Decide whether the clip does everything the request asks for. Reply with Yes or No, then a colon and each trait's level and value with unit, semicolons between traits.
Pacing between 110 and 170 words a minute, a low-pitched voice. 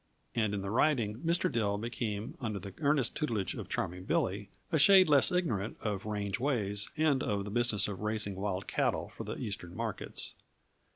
No: average, 180 wpm; low, 105 Hz